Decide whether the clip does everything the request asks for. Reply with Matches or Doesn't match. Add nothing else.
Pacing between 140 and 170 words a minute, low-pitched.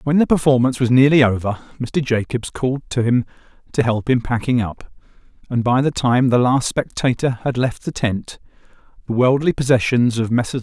Doesn't match